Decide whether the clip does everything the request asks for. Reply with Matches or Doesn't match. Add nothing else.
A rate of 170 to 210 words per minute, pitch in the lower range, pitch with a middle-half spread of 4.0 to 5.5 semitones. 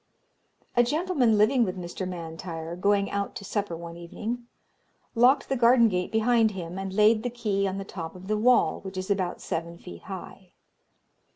Doesn't match